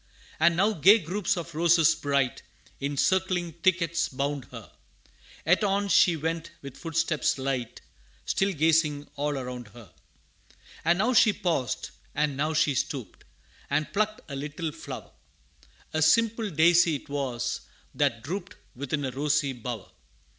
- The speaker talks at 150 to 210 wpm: No, average, 140 wpm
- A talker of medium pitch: Yes, medium, 155 Hz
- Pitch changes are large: No, average, 3.9 semitones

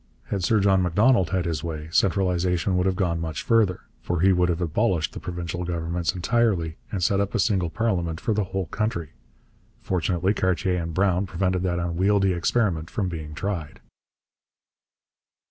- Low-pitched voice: Yes, very low, 90 Hz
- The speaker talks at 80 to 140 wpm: No, average, 165 wpm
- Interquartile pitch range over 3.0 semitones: No, narrow, 2.6 semitones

